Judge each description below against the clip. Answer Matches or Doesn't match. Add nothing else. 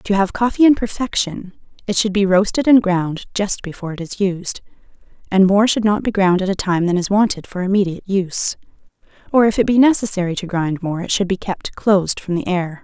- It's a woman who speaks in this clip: Matches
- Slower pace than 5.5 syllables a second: Doesn't match